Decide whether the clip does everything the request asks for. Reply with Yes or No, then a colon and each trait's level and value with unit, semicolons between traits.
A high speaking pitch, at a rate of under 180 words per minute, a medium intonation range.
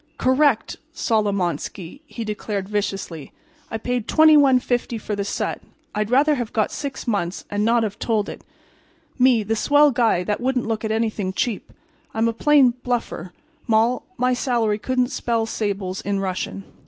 Yes: high, 225 Hz; average, 155 wpm; average, 3.5 semitones